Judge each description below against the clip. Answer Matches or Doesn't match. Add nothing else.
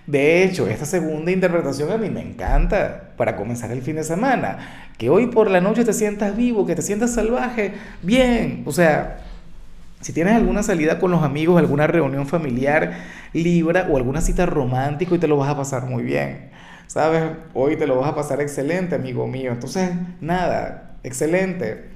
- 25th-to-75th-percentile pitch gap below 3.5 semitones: Doesn't match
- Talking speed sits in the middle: Matches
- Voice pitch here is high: Doesn't match